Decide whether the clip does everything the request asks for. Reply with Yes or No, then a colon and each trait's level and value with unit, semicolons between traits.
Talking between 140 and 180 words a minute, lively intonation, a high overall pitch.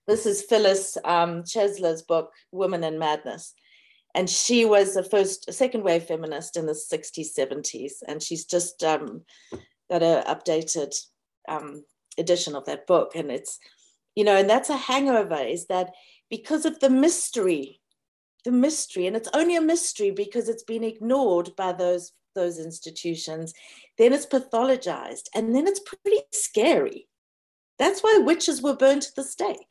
Yes: average, 160 wpm; wide, 8.2 semitones; high, 210 Hz